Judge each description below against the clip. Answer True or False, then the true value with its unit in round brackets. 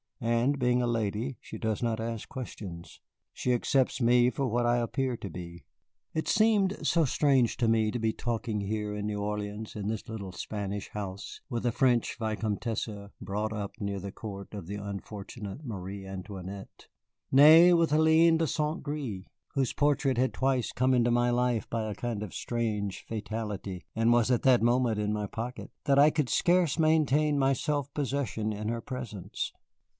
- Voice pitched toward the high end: False (115 Hz)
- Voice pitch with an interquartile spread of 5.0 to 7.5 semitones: False (4.3 semitones)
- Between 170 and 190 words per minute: True (180 wpm)